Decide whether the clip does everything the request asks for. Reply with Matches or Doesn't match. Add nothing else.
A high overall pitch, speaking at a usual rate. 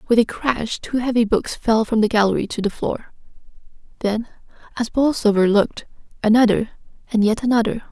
Matches